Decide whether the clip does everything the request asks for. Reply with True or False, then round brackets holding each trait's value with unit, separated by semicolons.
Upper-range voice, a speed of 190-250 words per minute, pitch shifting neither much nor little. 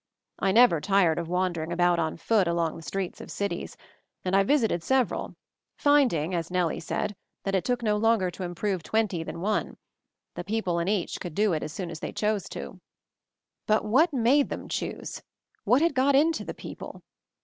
True (195 Hz; 195 wpm; 4.7 semitones)